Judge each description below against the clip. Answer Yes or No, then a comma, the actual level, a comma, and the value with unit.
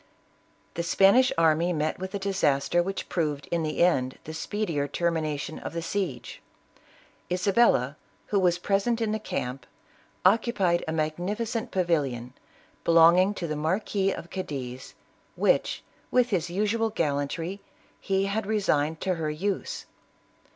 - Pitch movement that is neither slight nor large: Yes, average, 4.4 semitones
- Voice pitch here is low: No, medium, 175 Hz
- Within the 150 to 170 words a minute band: No, average, 140 wpm